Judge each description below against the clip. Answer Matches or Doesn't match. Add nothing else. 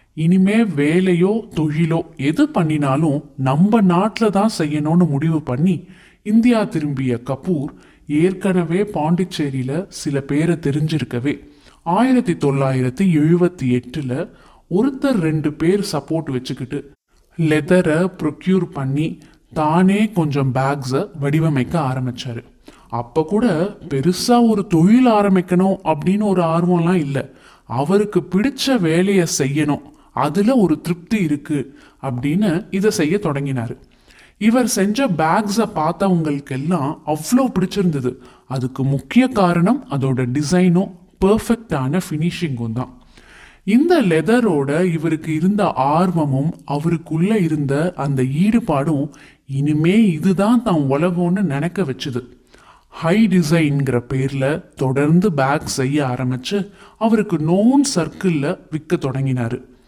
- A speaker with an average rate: Matches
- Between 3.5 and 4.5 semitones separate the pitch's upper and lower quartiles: Doesn't match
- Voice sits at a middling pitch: Matches